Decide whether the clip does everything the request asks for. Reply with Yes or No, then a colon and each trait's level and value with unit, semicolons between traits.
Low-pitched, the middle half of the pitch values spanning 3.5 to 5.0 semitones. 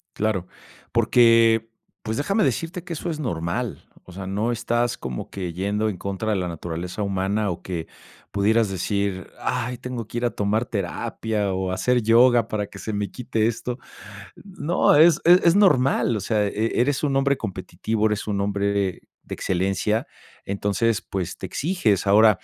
Yes: low, 110 Hz; average, 3.8 semitones